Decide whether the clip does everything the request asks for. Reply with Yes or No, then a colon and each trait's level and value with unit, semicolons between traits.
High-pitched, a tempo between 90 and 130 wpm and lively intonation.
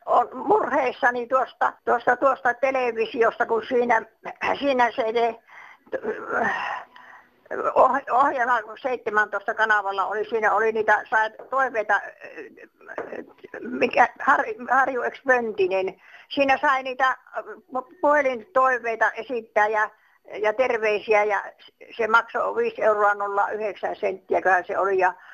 No: high, 230 Hz; average, 100 wpm; average, 3.5 semitones